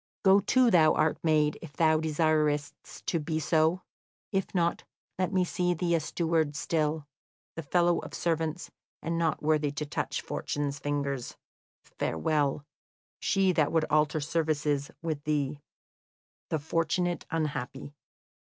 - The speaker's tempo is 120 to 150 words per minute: Yes, slow, 135 wpm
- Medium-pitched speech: Yes, medium, 155 Hz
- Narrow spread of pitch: Yes, narrow, 2.2 semitones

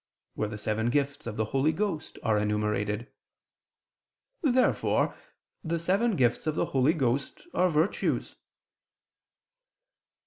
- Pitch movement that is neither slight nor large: No, wide, 7.3 semitones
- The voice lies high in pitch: No, low, 135 Hz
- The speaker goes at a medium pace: No, slow, 115 wpm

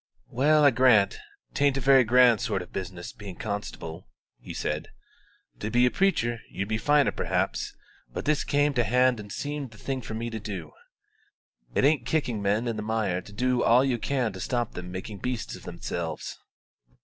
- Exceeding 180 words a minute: Yes, average, 190 wpm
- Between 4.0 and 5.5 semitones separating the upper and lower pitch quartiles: Yes, average, 4.3 semitones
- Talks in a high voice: No, low, 120 Hz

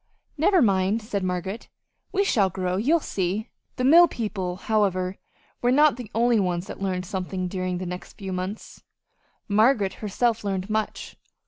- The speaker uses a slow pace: No, average, 155 wpm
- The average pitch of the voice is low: No, high, 200 Hz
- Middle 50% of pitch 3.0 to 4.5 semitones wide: Yes, average, 4.0 semitones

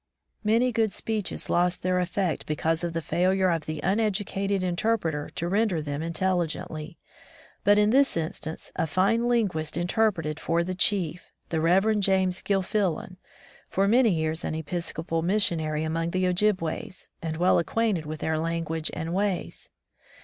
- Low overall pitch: No, medium, 180 Hz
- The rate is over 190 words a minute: No, average, 155 wpm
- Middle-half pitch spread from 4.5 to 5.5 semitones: No, average, 3.7 semitones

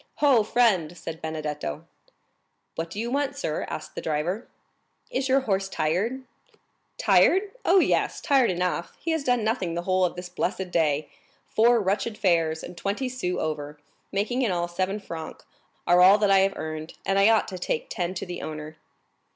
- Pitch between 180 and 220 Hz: Yes, medium, 185 Hz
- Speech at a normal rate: Yes, average, 175 wpm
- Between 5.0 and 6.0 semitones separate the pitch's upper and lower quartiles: Yes, wide, 5.6 semitones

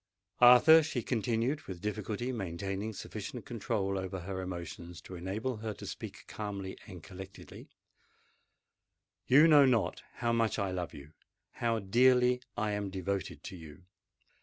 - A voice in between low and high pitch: No, low, 105 Hz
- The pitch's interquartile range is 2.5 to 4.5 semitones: Yes, average, 4.2 semitones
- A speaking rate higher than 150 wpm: No, slow, 135 wpm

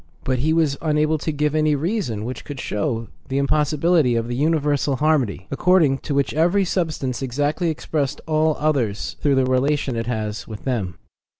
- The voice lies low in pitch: No, medium, 145 Hz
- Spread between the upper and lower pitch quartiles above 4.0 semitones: No, average, 3.7 semitones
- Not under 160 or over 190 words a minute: Yes, average, 175 wpm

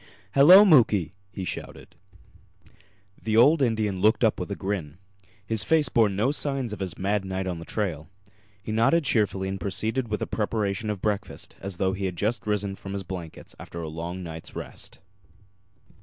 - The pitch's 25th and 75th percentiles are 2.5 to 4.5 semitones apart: Yes, average, 3.1 semitones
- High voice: No, low, 100 Hz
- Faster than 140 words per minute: Yes, average, 180 wpm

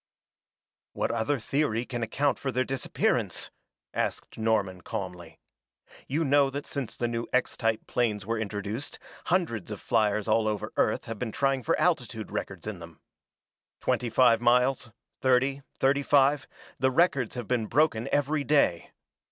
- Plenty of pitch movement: No, average, 3.8 semitones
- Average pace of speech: Yes, average, 150 wpm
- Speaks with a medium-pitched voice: No, low, 120 Hz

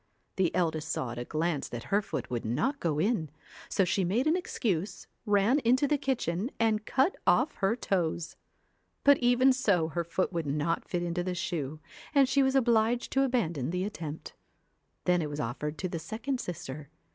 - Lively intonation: Yes, wide, 7.3 semitones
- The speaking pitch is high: No, medium, 180 Hz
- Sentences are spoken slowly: No, average, 180 wpm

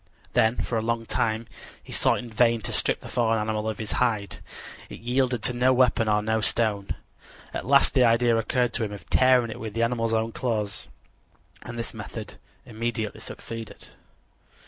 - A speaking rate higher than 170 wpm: Yes, average, 185 wpm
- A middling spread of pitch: No, narrow, 1.8 semitones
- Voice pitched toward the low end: Yes, low, 115 Hz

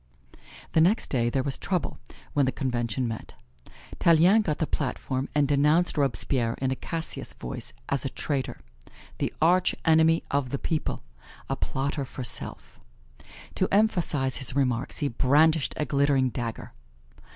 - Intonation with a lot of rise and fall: No, average, 3.7 semitones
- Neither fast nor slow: Yes, average, 150 wpm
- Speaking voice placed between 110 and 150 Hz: Yes, medium, 140 Hz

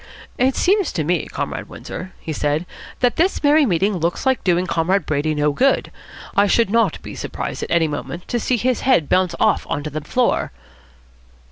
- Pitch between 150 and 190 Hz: Yes, medium, 185 Hz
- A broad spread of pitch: Yes, wide, 7.9 semitones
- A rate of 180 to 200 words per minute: Yes, average, 195 wpm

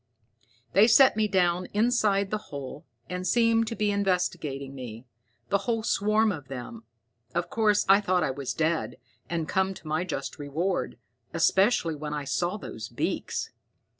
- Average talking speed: Yes, average, 160 wpm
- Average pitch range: No, wide, 5.7 semitones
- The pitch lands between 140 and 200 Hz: Yes, medium, 185 Hz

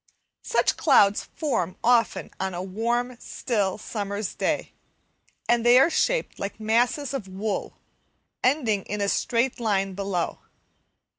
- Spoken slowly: Yes, slow, 125 wpm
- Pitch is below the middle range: No, high, 220 Hz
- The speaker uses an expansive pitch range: No, average, 3.7 semitones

